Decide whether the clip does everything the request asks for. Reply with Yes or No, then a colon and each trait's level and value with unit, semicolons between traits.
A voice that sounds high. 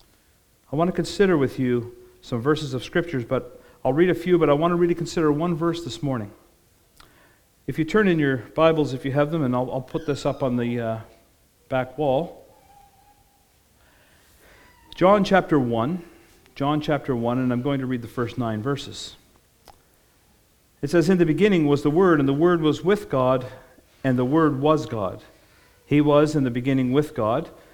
No: medium, 140 Hz